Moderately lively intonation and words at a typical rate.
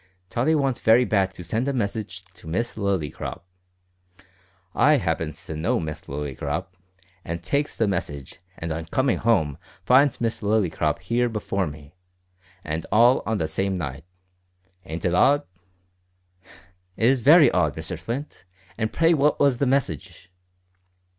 No: wide, 7.3 semitones; average, 145 wpm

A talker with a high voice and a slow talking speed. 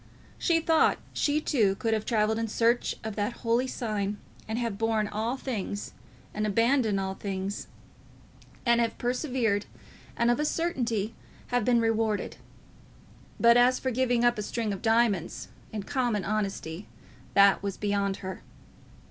No: high, 225 Hz; average, 150 wpm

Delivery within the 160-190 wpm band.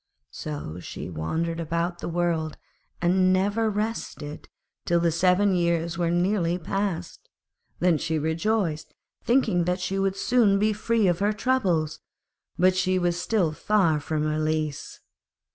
No: average, 140 wpm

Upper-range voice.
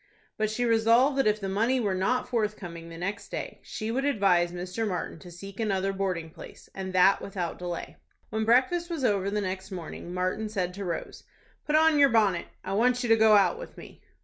Yes: high, 205 Hz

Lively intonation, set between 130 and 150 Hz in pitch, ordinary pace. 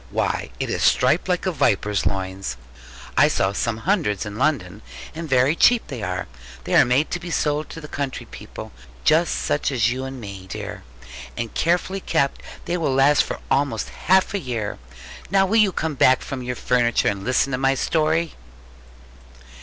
Yes: wide, 6.3 semitones; low, 135 Hz; average, 180 wpm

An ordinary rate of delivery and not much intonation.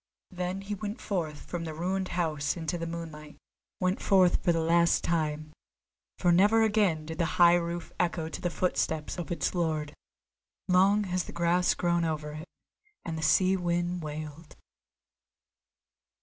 Yes: average, 160 wpm; narrow, 2.3 semitones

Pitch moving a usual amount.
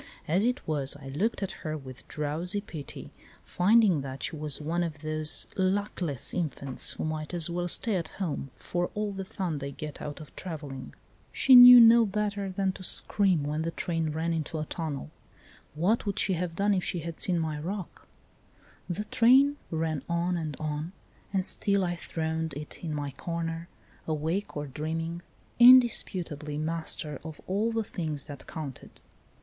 Yes: average, 4.0 semitones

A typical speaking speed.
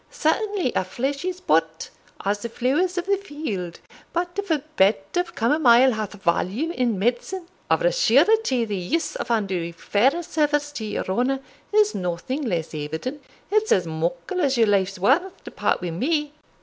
Yes: average, 170 wpm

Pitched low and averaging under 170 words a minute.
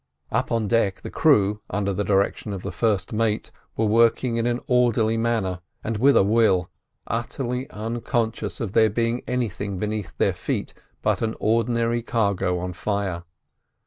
Yes: low, 110 Hz; average, 160 wpm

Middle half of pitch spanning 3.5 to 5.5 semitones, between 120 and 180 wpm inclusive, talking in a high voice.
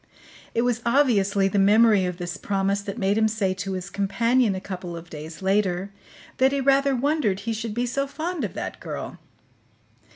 No: average, 4.1 semitones; average, 190 wpm; high, 205 Hz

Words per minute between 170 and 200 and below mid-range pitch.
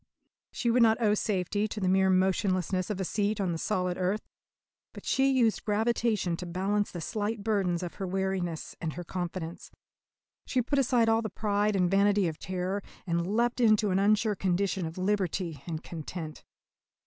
No: average, 180 wpm; high, 195 Hz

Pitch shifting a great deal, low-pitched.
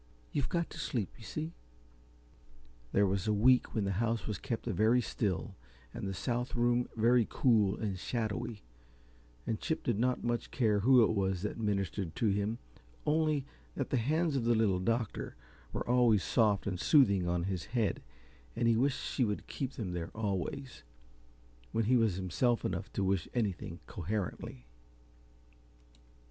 No: average, 3.9 semitones; low, 110 Hz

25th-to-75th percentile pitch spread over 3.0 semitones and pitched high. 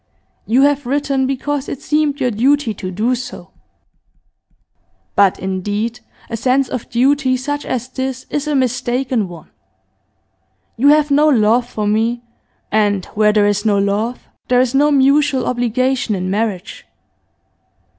Yes: average, 4.2 semitones; very high, 250 Hz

